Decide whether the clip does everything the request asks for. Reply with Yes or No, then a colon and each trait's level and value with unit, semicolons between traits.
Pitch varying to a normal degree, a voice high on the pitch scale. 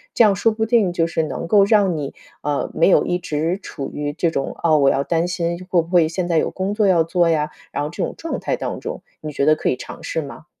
No: average, 3.4 semitones; medium, 170 Hz